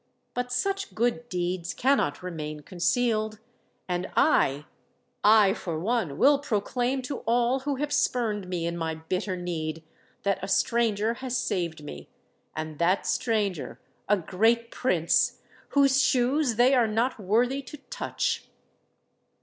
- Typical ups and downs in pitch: No, wide, 6.0 semitones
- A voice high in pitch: Yes, high, 215 Hz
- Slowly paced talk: Yes, slow, 130 wpm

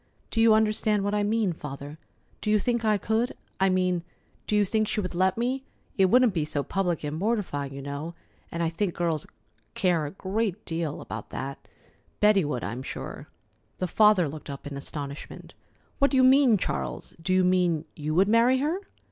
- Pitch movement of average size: No, wide, 5.7 semitones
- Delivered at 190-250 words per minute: Yes, average, 195 wpm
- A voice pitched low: No, medium, 185 Hz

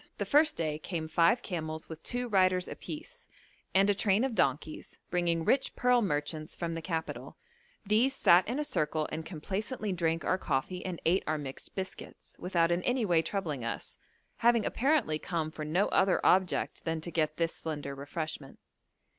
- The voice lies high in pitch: No, medium, 170 Hz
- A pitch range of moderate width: Yes, average, 4.6 semitones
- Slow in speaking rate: No, average, 175 wpm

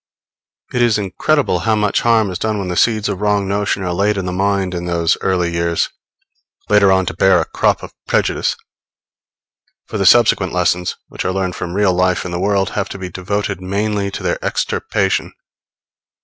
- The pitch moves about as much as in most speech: No, narrow, 2.3 semitones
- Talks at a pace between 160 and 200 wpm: Yes, average, 190 wpm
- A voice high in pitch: No, very low, 95 Hz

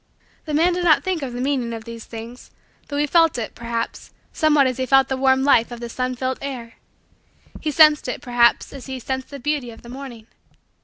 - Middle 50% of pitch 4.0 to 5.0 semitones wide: No, average, 3.3 semitones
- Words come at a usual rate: No, fast, 220 wpm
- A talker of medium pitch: No, very high, 260 Hz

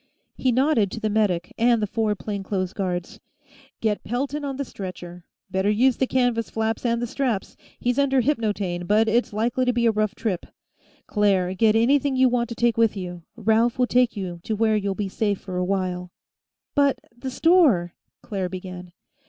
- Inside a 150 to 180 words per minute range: No, average, 190 wpm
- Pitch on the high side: Yes, high, 220 Hz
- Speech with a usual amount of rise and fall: Yes, average, 4.2 semitones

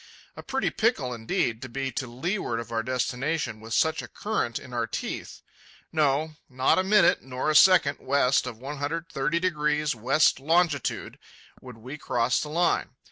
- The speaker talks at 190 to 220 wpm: No, average, 160 wpm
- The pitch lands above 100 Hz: Yes, medium, 140 Hz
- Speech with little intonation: No, average, 4.4 semitones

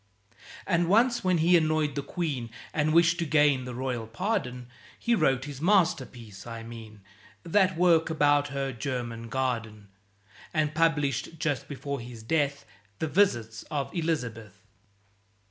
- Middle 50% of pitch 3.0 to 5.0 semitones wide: No, wide, 5.5 semitones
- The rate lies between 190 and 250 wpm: No, average, 140 wpm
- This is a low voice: No, medium, 145 Hz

